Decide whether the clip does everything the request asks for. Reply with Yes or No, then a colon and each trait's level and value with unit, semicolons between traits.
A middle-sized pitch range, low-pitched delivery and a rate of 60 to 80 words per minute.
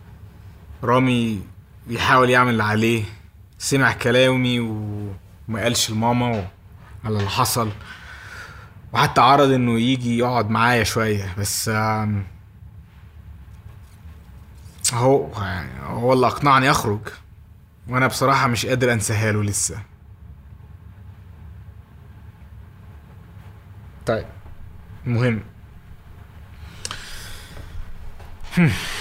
Yes: average, 3.6 semitones; low, 100 Hz; average, 70 wpm